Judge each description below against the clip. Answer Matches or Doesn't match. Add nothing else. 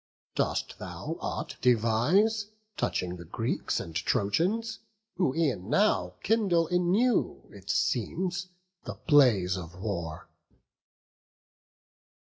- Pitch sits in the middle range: Matches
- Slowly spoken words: Matches